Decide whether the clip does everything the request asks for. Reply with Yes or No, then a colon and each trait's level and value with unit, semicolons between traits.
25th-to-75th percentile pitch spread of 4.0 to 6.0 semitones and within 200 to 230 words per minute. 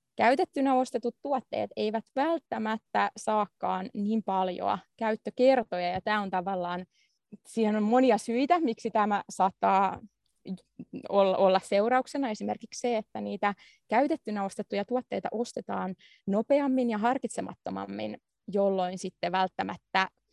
No: average, 4.3 semitones; average, 105 wpm